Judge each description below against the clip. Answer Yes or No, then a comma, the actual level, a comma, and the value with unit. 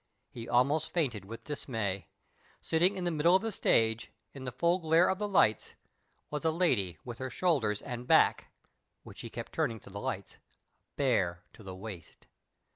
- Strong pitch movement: Yes, wide, 7.3 semitones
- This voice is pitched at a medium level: No, low, 125 Hz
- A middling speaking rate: Yes, average, 180 wpm